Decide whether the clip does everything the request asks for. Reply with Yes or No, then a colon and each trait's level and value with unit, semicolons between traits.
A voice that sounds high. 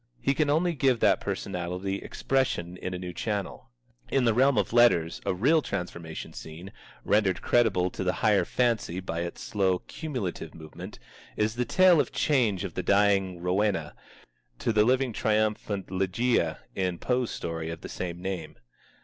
No: low, 100 Hz